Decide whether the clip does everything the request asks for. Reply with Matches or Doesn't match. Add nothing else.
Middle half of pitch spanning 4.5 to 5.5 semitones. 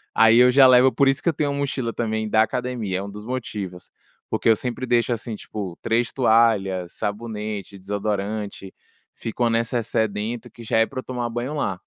Doesn't match